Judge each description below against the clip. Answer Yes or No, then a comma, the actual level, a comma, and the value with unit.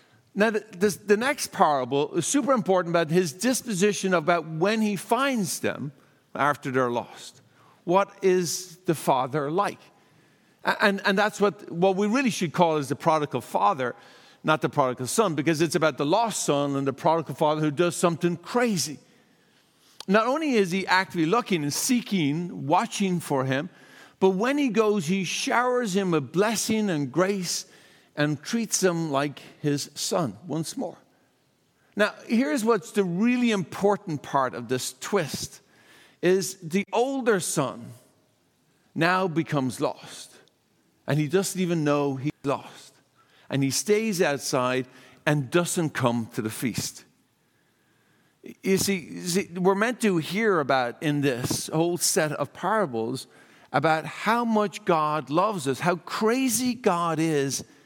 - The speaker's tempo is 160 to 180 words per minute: No, average, 150 wpm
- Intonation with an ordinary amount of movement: No, wide, 5.9 semitones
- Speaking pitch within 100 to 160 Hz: No, medium, 175 Hz